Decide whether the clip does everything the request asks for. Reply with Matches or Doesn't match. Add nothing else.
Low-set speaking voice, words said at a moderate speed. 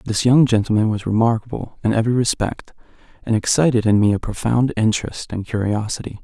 Matches